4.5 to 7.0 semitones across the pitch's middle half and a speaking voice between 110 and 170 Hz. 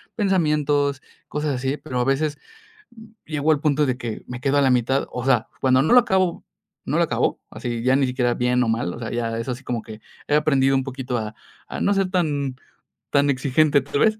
No: average, 3.2 semitones; low, 135 Hz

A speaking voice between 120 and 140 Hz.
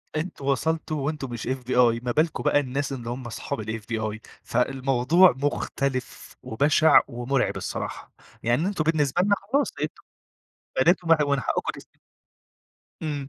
Yes: low, 135 Hz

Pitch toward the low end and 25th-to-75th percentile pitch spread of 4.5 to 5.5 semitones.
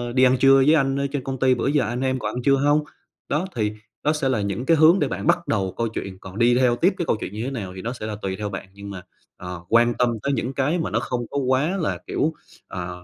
Yes: low, 125 Hz; average, 4.8 semitones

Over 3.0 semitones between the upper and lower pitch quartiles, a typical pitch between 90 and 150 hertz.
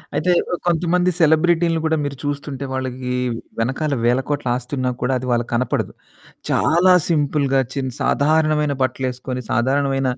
Yes: average, 3.6 semitones; medium, 140 Hz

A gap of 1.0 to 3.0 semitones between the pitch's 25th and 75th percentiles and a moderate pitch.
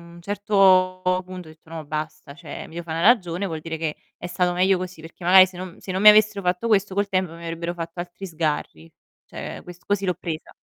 Yes: narrow, 2.4 semitones; medium, 180 Hz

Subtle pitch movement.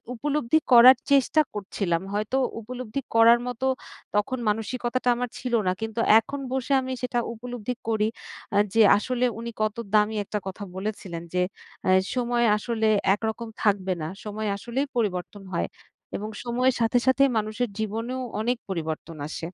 No: average, 3.1 semitones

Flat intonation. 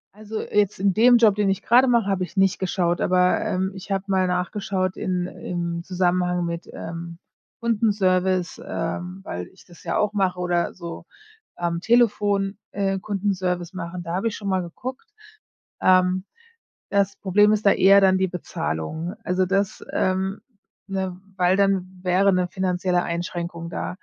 Yes: narrow, 1.9 semitones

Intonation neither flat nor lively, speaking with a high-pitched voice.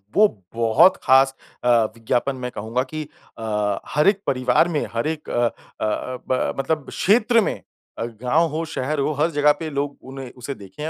No: average, 4.5 semitones; low, 135 Hz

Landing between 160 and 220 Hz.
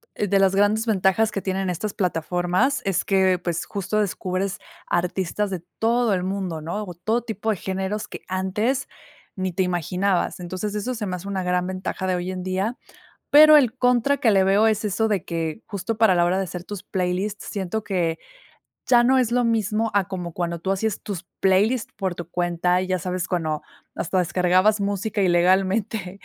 Yes: high, 190 Hz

